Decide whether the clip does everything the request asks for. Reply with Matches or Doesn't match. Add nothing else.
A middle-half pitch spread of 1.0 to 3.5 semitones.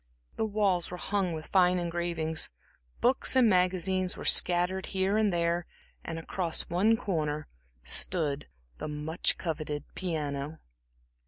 Matches